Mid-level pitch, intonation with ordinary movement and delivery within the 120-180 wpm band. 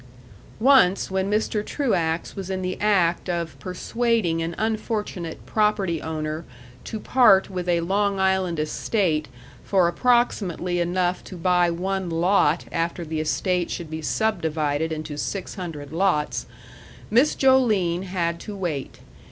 Yes: medium, 180 Hz; average, 3.5 semitones; slow, 135 wpm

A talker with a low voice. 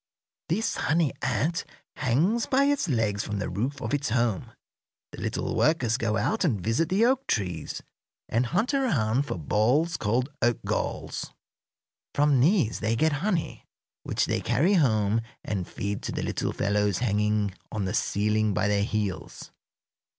Yes: low, 120 Hz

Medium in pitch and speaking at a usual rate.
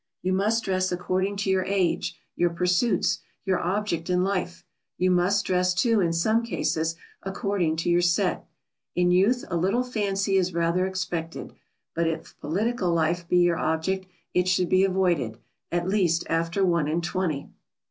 Yes: medium, 180 Hz; average, 165 wpm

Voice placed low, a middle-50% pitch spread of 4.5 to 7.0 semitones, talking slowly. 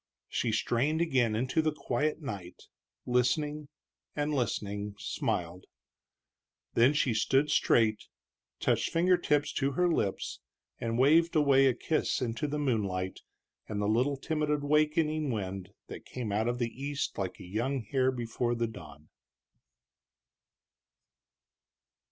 Yes: low, 125 Hz; wide, 5.4 semitones; slow, 130 wpm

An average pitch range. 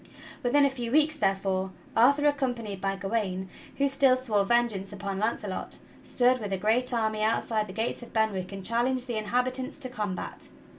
Yes: average, 4.3 semitones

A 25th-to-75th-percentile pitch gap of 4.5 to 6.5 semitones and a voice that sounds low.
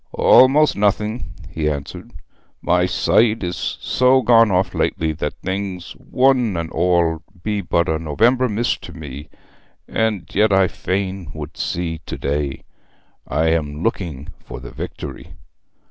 Yes: wide, 5.6 semitones; very low, 90 Hz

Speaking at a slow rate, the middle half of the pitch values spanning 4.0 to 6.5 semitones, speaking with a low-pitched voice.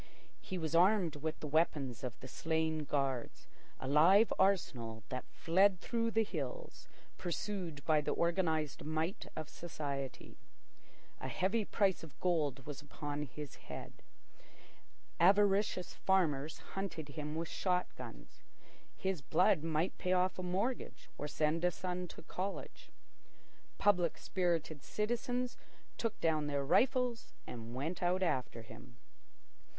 No: slow, 130 wpm; average, 4.4 semitones; medium, 165 Hz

